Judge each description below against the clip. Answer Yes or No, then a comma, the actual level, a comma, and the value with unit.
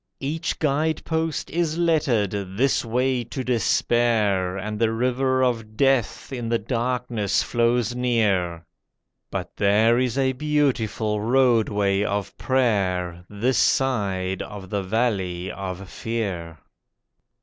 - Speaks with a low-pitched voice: Yes, low, 115 Hz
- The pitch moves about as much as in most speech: Yes, average, 4.5 semitones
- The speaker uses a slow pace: Yes, slow, 115 wpm